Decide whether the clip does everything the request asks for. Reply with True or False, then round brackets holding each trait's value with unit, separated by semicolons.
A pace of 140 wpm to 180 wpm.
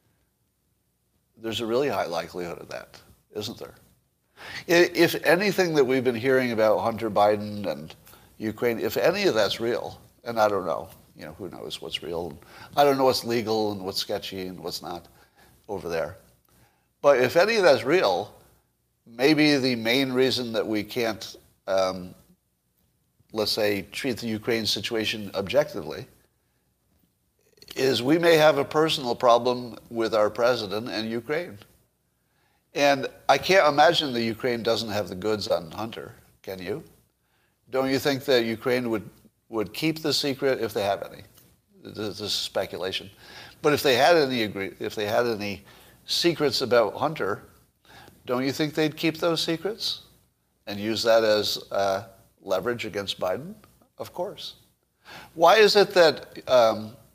True (155 wpm)